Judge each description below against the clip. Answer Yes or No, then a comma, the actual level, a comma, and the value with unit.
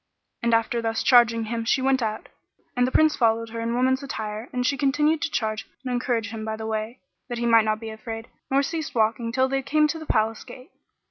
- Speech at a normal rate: No, fast, 240 wpm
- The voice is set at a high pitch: Yes, high, 235 Hz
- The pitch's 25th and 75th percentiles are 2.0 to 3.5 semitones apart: Yes, average, 2.8 semitones